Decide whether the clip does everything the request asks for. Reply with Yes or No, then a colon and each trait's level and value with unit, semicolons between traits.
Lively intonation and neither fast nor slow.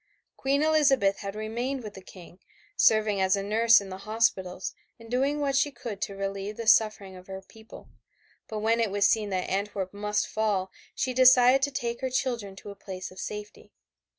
No: average, 3.7 semitones; average, 195 wpm